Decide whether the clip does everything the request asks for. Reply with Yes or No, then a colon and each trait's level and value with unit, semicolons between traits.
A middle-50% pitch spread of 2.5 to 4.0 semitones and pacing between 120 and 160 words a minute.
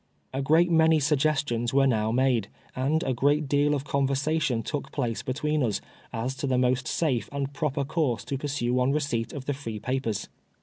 No: average, 2.9 semitones; average, 185 wpm